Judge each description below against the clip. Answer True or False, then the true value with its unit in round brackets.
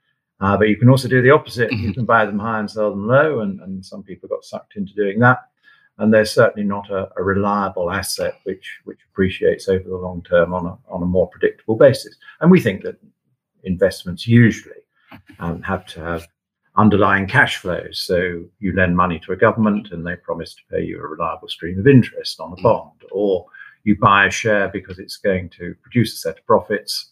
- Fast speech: True (210 wpm)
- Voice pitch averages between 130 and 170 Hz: False (105 Hz)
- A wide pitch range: True (7.0 semitones)